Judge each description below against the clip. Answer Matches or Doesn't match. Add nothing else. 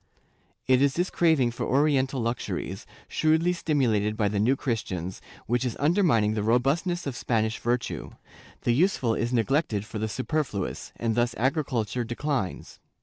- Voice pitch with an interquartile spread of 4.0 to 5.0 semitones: Matches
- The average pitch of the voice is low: Matches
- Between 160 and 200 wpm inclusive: Doesn't match